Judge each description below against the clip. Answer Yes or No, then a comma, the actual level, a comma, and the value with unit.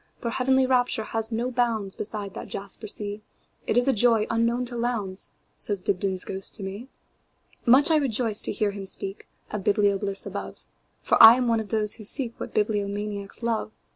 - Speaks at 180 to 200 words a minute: No, average, 160 wpm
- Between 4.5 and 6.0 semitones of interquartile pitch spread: No, average, 3.0 semitones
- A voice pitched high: Yes, high, 220 Hz